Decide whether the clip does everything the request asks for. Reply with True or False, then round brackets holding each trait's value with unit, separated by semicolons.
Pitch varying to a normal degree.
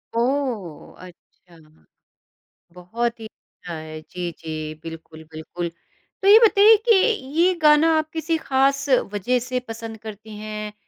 False (8.3 semitones)